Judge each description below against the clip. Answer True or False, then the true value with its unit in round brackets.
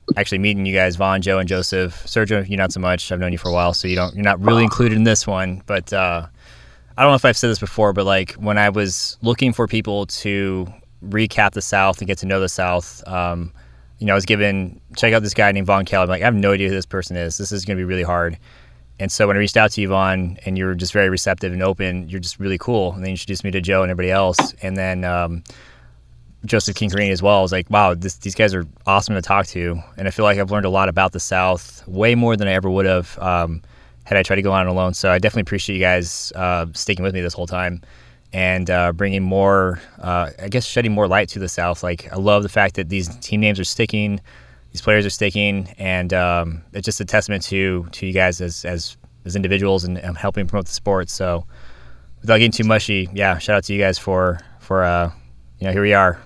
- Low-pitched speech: True (95 Hz)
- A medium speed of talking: False (260 wpm)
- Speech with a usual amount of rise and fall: False (2.2 semitones)